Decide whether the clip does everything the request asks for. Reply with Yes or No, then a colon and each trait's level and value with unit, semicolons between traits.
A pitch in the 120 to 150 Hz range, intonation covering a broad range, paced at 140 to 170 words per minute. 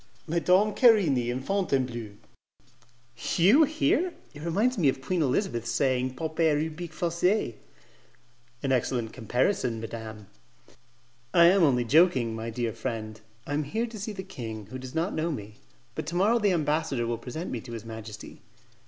Yes: medium, 140 Hz; wide, 7.3 semitones; average, 160 wpm